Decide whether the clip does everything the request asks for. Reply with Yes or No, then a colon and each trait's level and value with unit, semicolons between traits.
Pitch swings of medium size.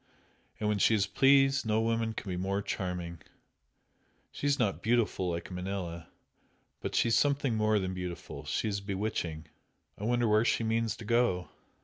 Yes: average, 4.0 semitones